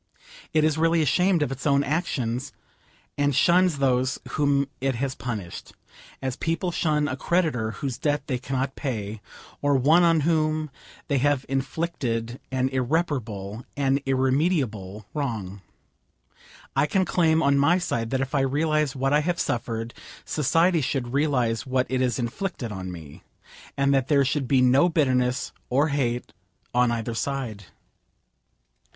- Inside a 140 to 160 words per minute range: Yes, average, 150 wpm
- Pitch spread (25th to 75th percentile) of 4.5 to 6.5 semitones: No, average, 3.6 semitones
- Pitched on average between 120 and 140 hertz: Yes, low, 135 Hz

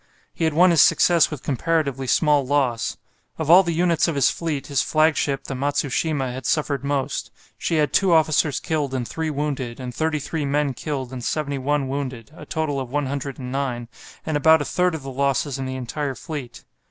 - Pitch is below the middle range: No, medium, 145 Hz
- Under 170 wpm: No, average, 190 wpm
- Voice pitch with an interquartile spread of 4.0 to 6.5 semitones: No, average, 2.9 semitones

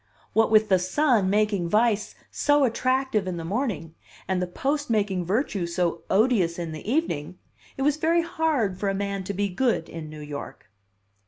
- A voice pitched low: No, high, 200 Hz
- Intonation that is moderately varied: No, wide, 6.3 semitones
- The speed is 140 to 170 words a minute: No, average, 185 wpm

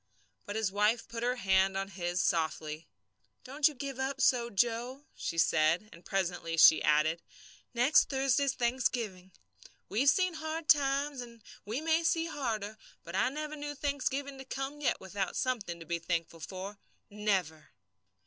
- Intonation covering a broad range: Yes, wide, 6.6 semitones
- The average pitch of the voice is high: Yes, high, 230 Hz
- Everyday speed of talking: Yes, average, 160 wpm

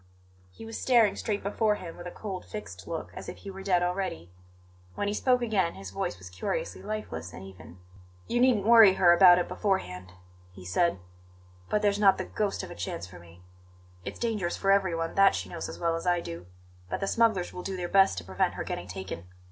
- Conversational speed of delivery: No, fast, 220 wpm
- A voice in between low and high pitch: Yes, medium, 180 Hz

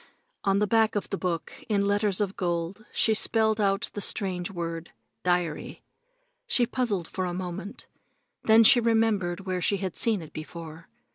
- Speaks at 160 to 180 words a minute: Yes, average, 165 wpm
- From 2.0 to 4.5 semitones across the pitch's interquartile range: Yes, average, 3.5 semitones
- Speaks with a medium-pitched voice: No, high, 195 Hz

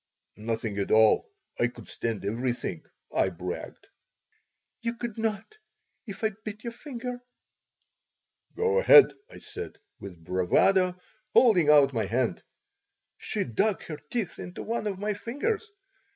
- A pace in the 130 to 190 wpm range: Yes, slow, 135 wpm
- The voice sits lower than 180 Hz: No, high, 195 Hz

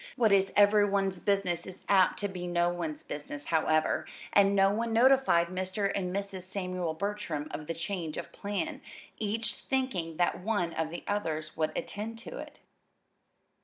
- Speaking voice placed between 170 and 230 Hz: Yes, high, 190 Hz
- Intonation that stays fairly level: No, average, 3.2 semitones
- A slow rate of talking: No, average, 165 wpm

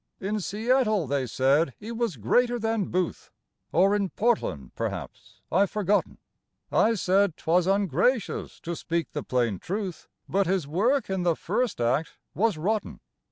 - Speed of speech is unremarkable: Yes, average, 150 wpm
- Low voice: No, high, 190 Hz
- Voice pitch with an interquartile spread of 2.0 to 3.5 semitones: No, average, 4.8 semitones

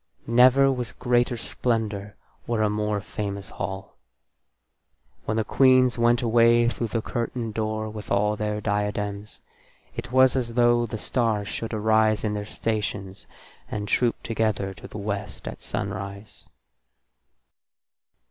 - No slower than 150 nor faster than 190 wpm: No, slow, 135 wpm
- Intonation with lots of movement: No, narrow, 2.4 semitones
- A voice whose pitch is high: No, low, 110 Hz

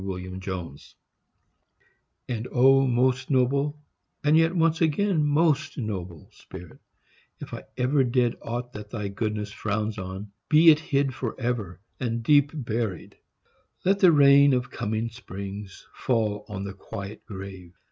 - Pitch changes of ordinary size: No, wide, 5.8 semitones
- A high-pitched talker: No, low, 120 Hz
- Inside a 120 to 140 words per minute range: Yes, slow, 135 wpm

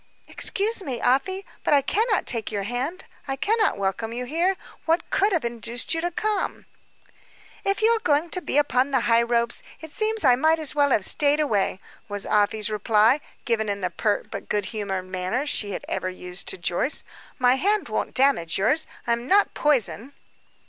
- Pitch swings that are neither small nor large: No, wide, 7.4 semitones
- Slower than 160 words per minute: No, average, 190 wpm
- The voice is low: No, very high, 255 Hz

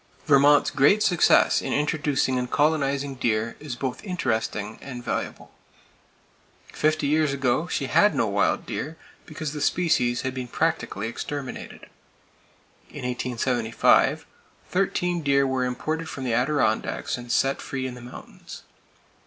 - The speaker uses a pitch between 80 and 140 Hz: Yes, low, 135 Hz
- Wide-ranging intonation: No, average, 3.7 semitones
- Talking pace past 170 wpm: No, slow, 135 wpm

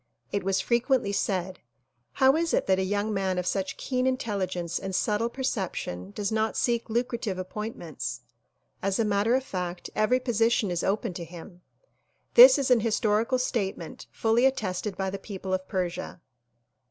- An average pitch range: Yes, average, 4.0 semitones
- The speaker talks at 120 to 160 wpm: No, average, 170 wpm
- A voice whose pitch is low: No, high, 205 Hz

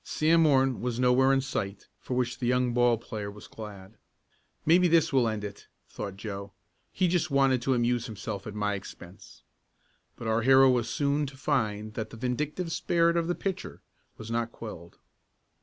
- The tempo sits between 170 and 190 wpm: Yes, average, 180 wpm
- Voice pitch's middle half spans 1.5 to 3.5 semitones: No, average, 4.2 semitones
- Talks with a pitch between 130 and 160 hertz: No, low, 120 Hz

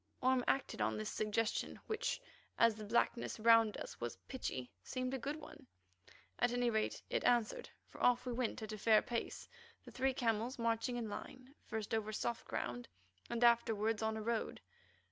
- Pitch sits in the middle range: No, high, 230 Hz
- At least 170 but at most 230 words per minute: Yes, average, 180 wpm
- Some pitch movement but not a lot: No, narrow, 2.3 semitones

